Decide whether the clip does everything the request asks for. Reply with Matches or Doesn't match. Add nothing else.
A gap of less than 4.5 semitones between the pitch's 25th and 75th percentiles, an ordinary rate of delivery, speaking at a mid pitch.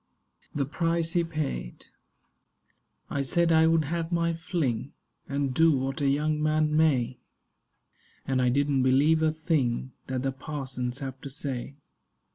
Matches